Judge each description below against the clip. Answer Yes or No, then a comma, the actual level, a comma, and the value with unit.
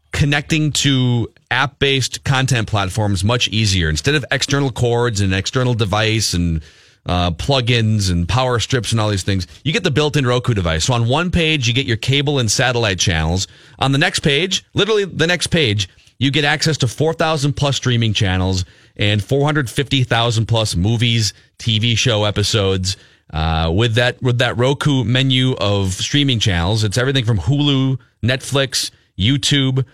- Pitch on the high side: No, low, 120 Hz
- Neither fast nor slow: Yes, average, 170 wpm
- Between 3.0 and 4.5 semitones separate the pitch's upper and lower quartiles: No, average, 4.9 semitones